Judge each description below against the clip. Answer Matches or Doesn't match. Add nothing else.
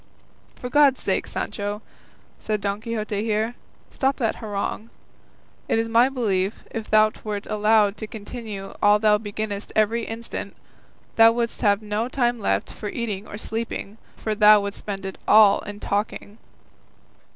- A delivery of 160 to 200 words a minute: Doesn't match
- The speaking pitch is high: Matches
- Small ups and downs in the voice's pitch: Matches